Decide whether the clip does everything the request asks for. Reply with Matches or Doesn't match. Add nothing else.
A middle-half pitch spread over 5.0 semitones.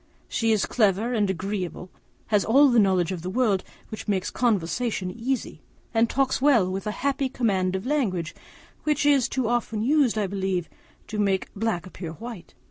Doesn't match